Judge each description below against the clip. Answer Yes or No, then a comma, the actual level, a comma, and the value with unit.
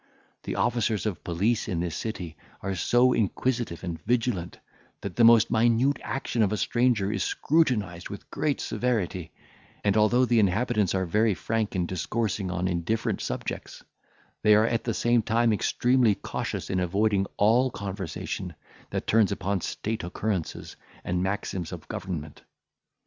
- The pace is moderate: Yes, average, 150 wpm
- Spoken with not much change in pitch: No, average, 4.1 semitones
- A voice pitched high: No, low, 105 Hz